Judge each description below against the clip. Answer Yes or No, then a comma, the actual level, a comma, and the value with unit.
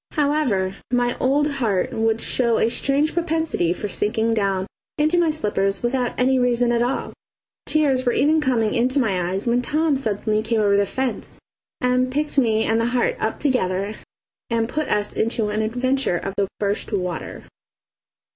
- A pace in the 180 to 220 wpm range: No, average, 170 wpm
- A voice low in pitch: No, high, 240 Hz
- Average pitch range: Yes, average, 4.3 semitones